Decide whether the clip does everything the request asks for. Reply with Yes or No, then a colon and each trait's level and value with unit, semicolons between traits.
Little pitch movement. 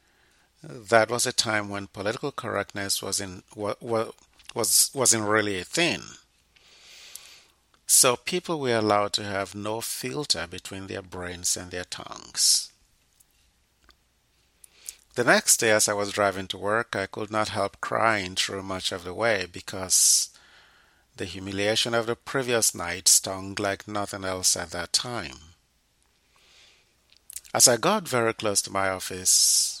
No: average, 3.2 semitones